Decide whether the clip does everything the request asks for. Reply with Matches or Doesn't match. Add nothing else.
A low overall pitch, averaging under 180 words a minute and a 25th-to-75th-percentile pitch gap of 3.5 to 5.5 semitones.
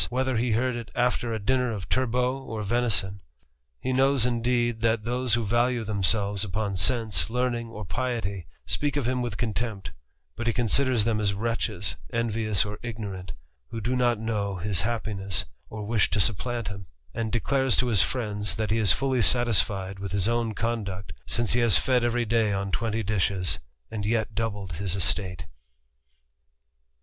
Doesn't match